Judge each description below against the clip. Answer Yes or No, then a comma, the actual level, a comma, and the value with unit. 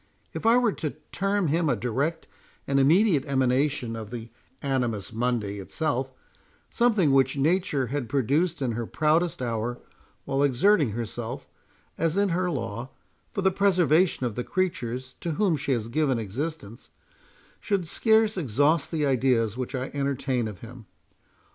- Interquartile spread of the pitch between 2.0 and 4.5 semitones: No, wide, 5.5 semitones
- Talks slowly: No, average, 150 wpm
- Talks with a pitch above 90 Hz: Yes, medium, 140 Hz